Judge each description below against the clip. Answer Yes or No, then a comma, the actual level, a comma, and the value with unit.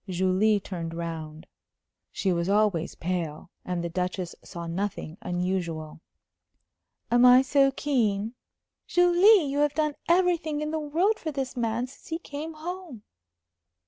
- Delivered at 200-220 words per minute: No, average, 140 wpm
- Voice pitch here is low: No, high, 220 Hz